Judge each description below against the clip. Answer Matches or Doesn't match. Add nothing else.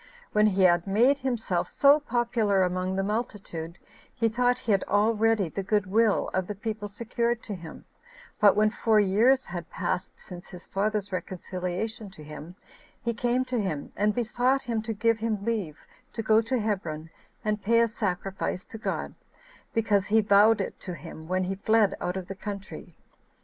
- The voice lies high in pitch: Matches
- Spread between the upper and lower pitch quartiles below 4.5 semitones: Matches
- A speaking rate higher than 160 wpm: Matches